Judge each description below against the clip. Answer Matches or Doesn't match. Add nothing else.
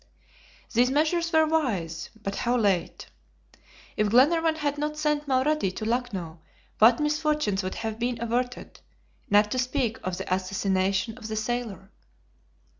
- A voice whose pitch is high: Matches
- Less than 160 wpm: Matches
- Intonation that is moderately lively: Doesn't match